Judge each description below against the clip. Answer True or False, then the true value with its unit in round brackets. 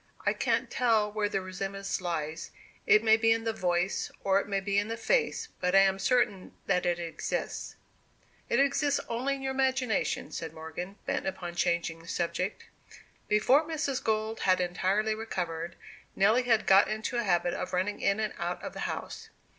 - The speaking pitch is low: False (200 Hz)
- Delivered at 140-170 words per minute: False (185 wpm)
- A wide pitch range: False (4.1 semitones)